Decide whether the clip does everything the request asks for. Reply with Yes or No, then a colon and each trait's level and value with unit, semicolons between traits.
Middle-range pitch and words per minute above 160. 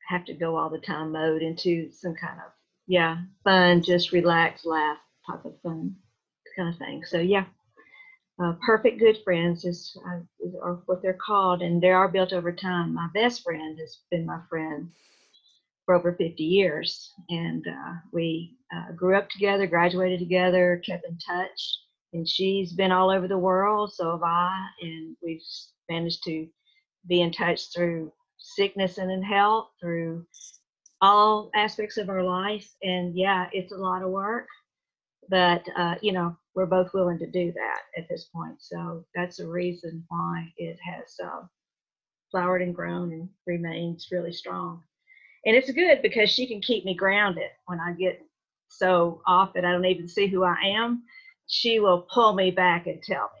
Yes: medium, 180 Hz; average, 175 wpm